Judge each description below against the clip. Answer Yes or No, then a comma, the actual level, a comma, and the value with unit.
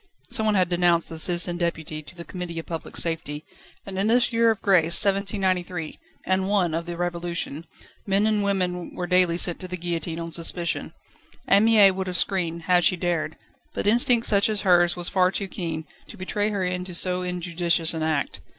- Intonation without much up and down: Yes, narrow, 2.3 semitones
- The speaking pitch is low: No, medium, 180 Hz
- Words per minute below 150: No, average, 195 wpm